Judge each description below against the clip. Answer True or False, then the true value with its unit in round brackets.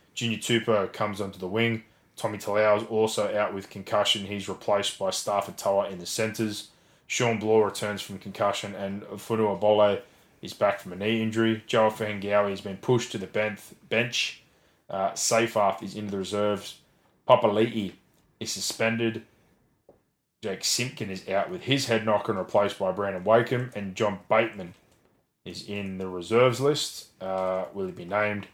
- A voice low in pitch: True (105 Hz)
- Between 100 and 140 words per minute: False (165 wpm)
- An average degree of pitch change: False (2.0 semitones)